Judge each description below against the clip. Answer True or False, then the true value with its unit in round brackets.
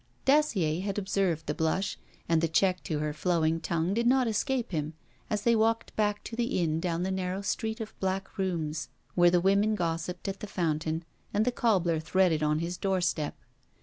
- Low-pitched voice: False (185 Hz)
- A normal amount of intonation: True (4.2 semitones)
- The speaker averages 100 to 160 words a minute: False (190 wpm)